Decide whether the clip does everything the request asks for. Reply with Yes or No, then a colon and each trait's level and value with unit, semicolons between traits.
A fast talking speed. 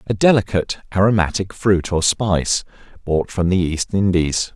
No: average, 145 wpm